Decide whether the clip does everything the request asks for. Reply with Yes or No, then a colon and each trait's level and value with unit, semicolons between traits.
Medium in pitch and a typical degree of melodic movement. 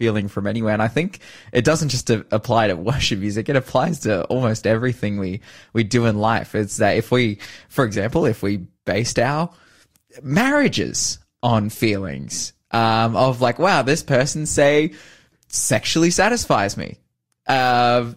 No: low, 115 Hz; average, 3.8 semitones